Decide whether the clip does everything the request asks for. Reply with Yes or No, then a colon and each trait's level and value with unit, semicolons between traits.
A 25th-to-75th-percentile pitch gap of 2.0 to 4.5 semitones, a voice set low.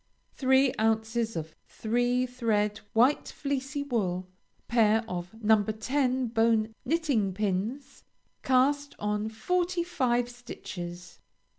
No: average, 3.9 semitones; high, 230 Hz